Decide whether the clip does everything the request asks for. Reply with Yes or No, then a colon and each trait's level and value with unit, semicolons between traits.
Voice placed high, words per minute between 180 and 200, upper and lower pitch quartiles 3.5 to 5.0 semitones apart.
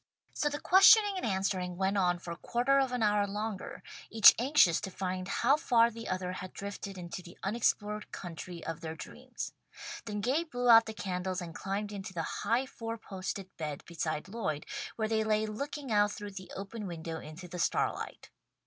Yes: high, 200 Hz; average, 185 wpm; average, 4.0 semitones